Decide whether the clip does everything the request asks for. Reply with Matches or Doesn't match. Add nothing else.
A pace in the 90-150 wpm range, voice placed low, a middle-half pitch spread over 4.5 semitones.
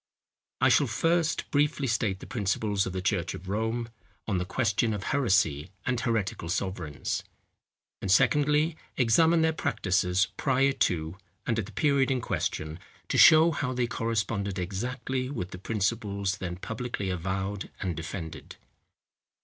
Matches